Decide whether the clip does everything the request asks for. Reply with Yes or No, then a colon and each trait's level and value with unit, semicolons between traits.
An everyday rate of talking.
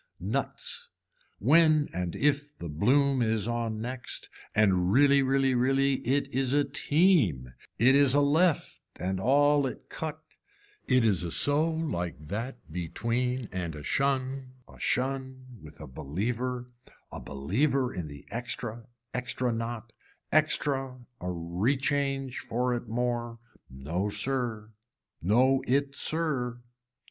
No: slow, 130 wpm